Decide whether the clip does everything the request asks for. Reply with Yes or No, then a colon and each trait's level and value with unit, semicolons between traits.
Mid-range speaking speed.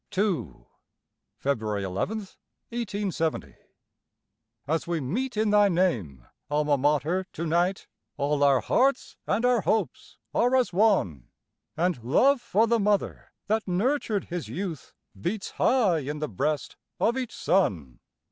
No: slow, 130 wpm